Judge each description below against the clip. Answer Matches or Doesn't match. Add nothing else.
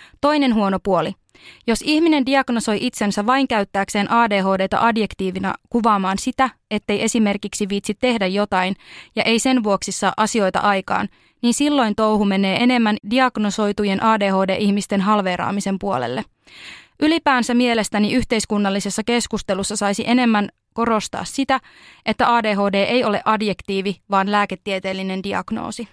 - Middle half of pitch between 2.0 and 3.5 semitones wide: Matches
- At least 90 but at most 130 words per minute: Matches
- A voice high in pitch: Matches